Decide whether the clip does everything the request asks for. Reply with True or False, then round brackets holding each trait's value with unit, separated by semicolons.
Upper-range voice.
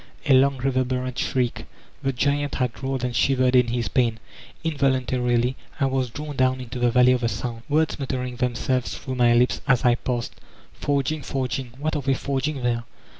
False (130 Hz)